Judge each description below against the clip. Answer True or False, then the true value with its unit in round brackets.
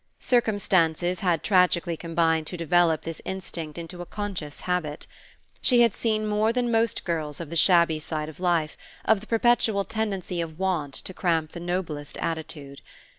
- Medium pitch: True (175 Hz)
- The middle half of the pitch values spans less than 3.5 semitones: False (3.8 semitones)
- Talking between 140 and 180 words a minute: True (165 wpm)